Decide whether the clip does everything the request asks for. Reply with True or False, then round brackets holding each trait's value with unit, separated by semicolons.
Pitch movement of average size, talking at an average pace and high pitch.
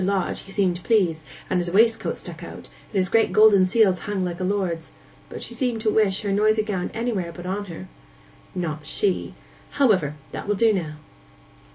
True (3.2 semitones; 190 wpm; 195 Hz)